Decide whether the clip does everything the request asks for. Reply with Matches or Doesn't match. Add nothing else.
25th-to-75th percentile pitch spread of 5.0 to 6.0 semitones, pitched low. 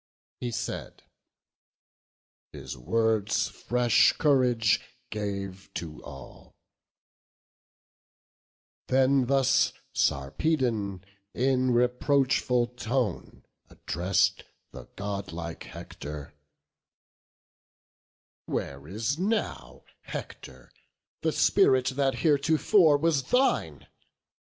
Matches